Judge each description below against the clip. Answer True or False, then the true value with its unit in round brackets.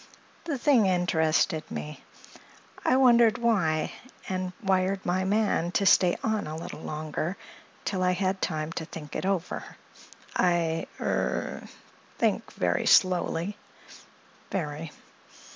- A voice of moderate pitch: True (180 Hz)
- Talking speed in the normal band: False (110 wpm)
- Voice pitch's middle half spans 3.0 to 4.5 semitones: True (3.5 semitones)